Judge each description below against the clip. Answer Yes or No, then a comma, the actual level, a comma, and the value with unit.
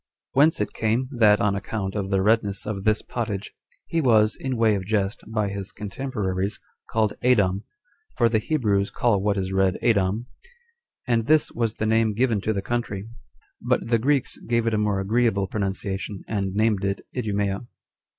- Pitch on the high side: No, low, 105 Hz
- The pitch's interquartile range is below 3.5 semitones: Yes, average, 2.8 semitones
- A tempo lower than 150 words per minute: No, average, 175 wpm